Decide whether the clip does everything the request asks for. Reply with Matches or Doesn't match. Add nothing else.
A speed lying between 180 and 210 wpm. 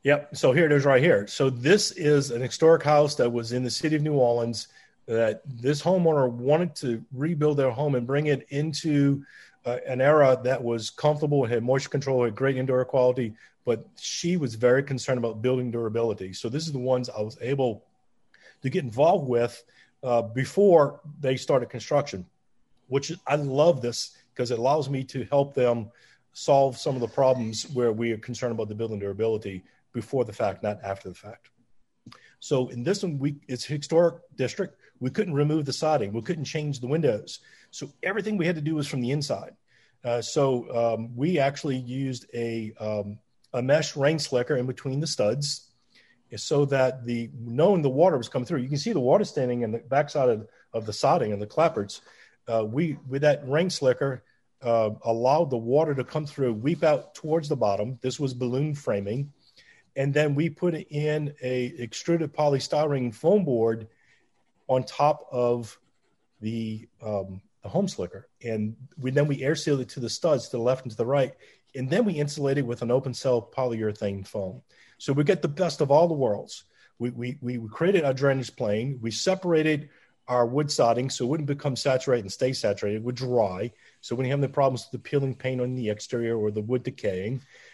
Matches